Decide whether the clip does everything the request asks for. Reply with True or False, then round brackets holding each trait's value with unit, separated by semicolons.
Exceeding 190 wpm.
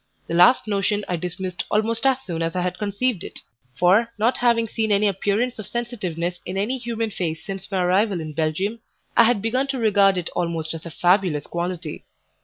True (200 wpm)